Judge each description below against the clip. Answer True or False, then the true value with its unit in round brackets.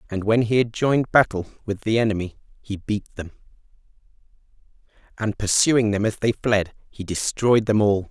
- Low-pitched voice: True (110 Hz)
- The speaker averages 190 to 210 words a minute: False (165 wpm)